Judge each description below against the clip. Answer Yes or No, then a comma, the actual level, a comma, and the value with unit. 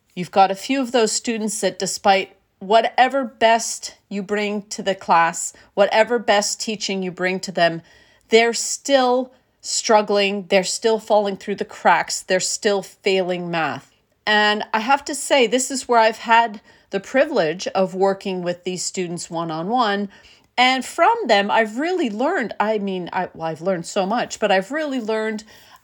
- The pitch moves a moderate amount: Yes, average, 3.4 semitones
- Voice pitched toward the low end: No, high, 210 Hz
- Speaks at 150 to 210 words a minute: Yes, average, 170 wpm